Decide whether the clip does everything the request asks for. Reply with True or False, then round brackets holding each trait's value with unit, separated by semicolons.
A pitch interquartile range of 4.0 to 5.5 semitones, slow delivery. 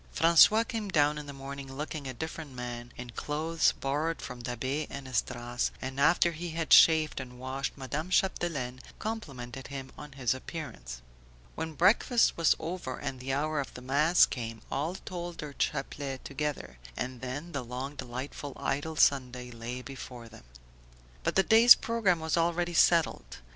False (4.3 semitones; 165 wpm)